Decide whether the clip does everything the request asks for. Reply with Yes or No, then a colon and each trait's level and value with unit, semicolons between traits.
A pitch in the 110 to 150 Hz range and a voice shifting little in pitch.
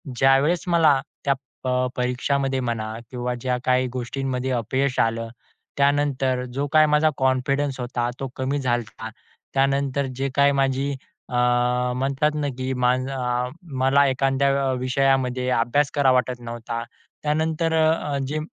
Yes: low, 135 Hz; narrow, 1.9 semitones